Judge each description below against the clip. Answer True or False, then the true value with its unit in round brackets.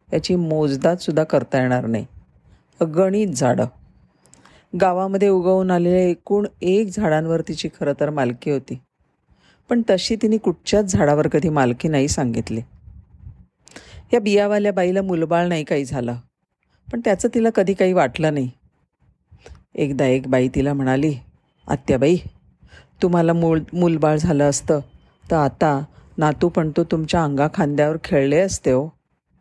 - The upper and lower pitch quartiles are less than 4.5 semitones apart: False (5.1 semitones)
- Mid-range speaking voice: True (160 Hz)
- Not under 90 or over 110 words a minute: False (125 wpm)